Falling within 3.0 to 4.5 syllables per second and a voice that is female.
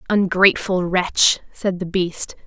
Yes: 3.9 syllables/s; female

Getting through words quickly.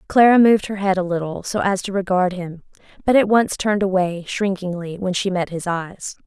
Yes: fast, 210 wpm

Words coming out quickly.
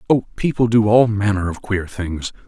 No: average, 195 wpm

